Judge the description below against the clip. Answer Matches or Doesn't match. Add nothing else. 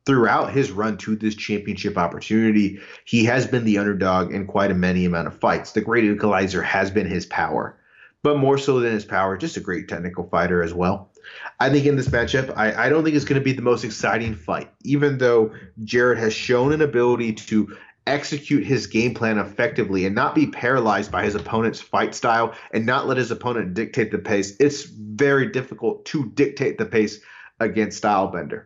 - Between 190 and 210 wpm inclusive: Matches